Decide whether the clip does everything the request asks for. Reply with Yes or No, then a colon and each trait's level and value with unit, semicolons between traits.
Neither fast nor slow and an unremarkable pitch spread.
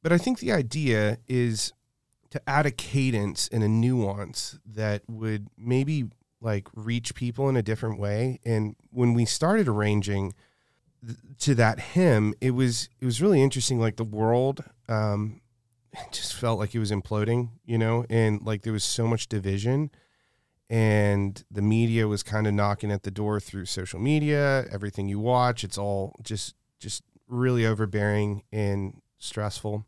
Yes: average, 165 wpm; average, 3.1 semitones